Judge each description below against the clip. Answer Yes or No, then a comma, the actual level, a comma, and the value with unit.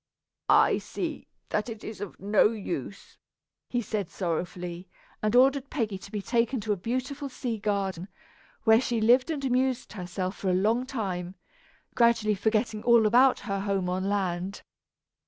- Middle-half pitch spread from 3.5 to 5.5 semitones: Yes, average, 3.9 semitones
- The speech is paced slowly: No, average, 155 wpm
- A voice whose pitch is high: Yes, high, 215 Hz